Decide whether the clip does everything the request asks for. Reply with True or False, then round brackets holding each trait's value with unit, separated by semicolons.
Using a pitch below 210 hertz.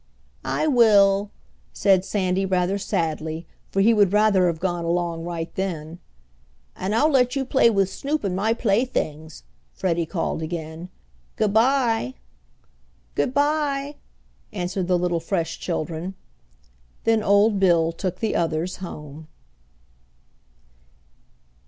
True (190 Hz)